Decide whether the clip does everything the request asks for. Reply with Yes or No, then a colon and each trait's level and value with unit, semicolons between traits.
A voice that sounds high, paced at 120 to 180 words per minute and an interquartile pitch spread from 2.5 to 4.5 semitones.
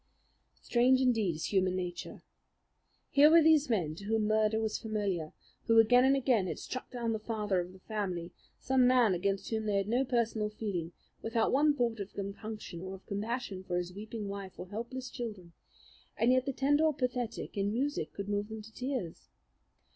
No: high, 220 Hz; average, 190 wpm; average, 4.0 semitones